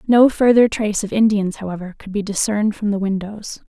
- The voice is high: Yes, high, 205 Hz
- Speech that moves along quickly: No, average, 195 wpm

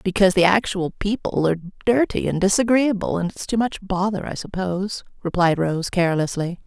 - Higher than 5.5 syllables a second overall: No, 5.4 syllables/s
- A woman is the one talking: Yes, female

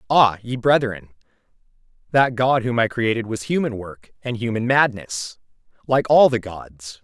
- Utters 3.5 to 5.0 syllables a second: Yes, 4.4 syllables/s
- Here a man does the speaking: Yes, male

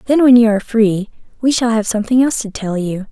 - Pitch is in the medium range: No, high, 225 Hz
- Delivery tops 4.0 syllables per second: Yes, 6.5 syllables/s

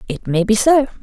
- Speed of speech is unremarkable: No, fast, 235 wpm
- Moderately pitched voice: No, high, 225 Hz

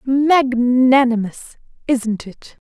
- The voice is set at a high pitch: Yes, very high, 250 Hz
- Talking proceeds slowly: Yes, slow, 70 wpm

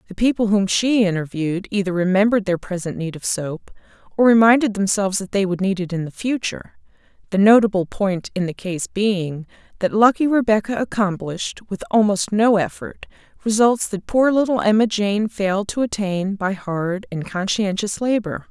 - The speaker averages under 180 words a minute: Yes, average, 170 wpm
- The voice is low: No, high, 200 Hz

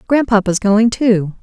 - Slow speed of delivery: Yes, slow, 125 wpm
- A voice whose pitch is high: Yes, high, 215 Hz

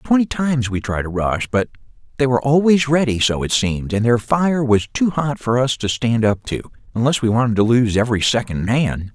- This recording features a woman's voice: No, male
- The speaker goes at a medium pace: No, fast, 210 wpm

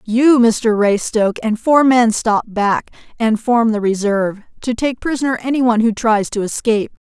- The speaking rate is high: No, average, 180 wpm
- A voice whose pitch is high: Yes, high, 225 Hz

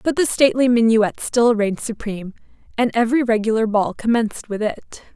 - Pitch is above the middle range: Yes, high, 225 Hz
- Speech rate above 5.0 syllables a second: Yes, 5.8 syllables/s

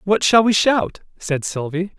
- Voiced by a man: Yes, male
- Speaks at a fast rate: No, average, 180 wpm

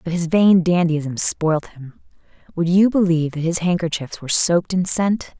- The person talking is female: Yes, female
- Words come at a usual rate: Yes, average, 180 wpm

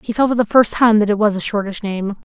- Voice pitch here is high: Yes, high, 210 Hz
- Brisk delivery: Yes, fast, 305 wpm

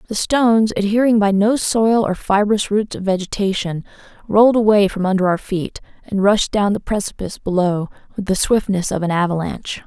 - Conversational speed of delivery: Yes, average, 175 wpm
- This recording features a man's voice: No, female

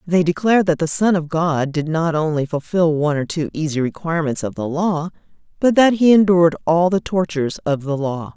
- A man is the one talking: No, female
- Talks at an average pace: No, fast, 210 wpm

